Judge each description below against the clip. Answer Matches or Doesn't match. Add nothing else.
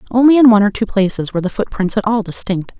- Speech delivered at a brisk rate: Matches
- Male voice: Doesn't match